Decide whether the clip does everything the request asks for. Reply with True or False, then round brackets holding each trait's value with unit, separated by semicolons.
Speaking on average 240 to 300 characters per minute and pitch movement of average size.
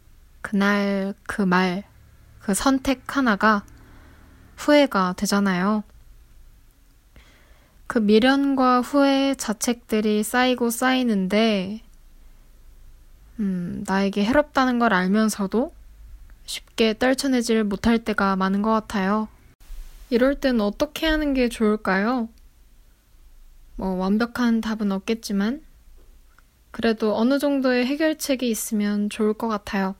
False (215 characters per minute; 4.0 semitones)